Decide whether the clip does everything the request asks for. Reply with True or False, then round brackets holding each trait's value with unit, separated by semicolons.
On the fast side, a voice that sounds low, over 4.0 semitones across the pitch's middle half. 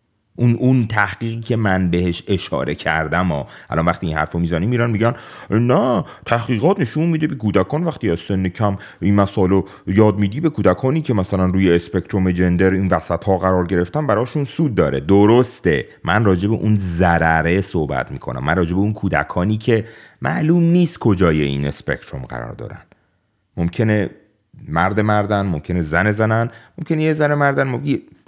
True (170 wpm; 100 Hz; 4.5 semitones)